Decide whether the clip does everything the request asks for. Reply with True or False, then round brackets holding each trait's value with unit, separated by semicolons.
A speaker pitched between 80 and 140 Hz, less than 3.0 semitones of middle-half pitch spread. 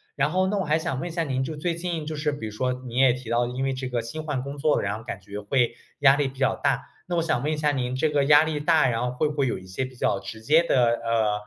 False (135 Hz; 4.1 semitones)